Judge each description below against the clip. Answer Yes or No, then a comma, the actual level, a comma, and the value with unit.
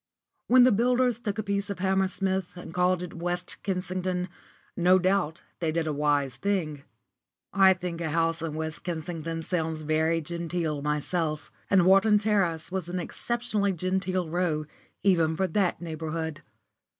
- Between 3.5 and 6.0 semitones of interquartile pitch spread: No, average, 3.1 semitones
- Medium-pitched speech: Yes, medium, 175 Hz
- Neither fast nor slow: Yes, average, 155 wpm